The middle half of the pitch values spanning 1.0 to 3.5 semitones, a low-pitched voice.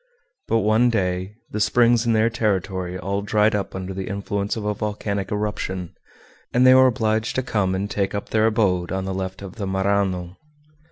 Yes: narrow, 2.4 semitones; low, 100 Hz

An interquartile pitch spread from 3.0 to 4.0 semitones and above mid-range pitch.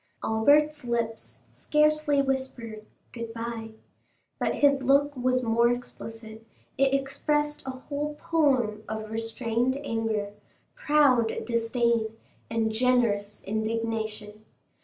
Yes: average, 3.6 semitones; high, 235 Hz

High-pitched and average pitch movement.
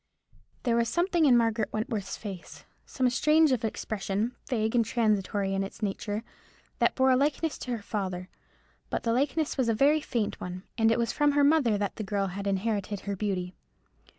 Yes: high, 225 Hz; average, 4.5 semitones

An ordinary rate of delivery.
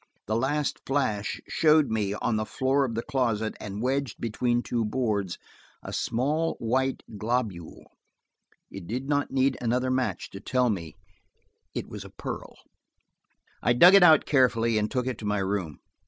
Yes: average, 165 wpm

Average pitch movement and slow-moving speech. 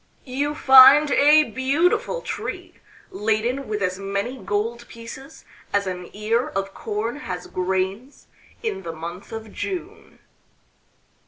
No: wide, 5.9 semitones; slow, 120 wpm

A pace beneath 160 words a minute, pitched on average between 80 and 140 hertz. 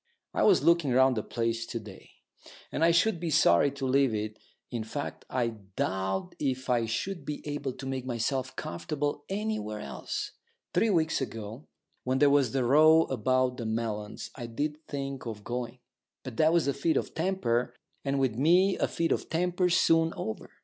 No: average, 185 wpm; low, 135 Hz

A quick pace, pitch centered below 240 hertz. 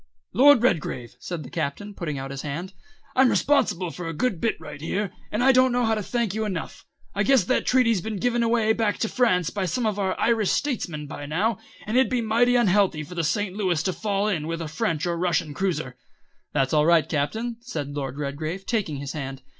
Yes: fast, 225 wpm; high, 190 Hz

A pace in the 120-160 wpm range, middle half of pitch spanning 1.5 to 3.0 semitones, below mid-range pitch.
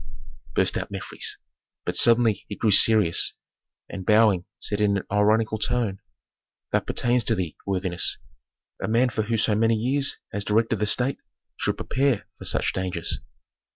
Yes: average, 155 wpm; narrow, 2.4 semitones; low, 110 Hz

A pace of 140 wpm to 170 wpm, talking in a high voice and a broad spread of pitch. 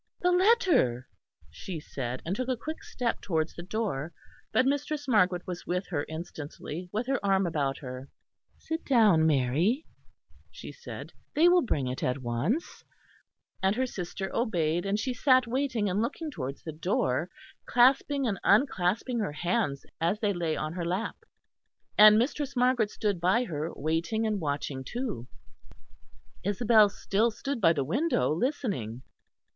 Yes: average, 155 wpm; high, 195 Hz; wide, 7.7 semitones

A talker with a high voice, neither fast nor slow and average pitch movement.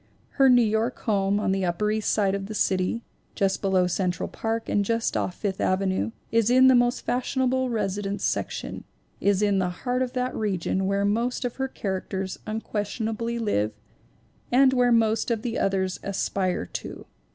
Yes: high, 210 Hz; average, 175 wpm; average, 3.6 semitones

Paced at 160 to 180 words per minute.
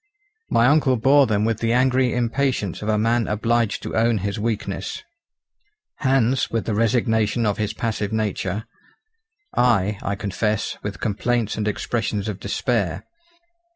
No: average, 145 wpm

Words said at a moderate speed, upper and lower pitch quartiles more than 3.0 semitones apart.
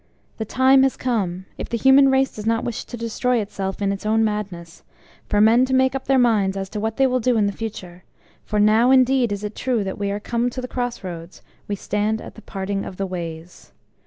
No: fast, 240 wpm; average, 4.0 semitones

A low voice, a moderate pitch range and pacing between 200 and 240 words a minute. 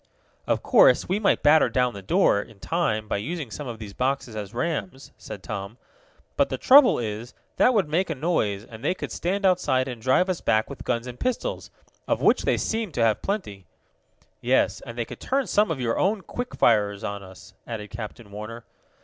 No: low, 120 Hz; wide, 8.8 semitones; fast, 205 wpm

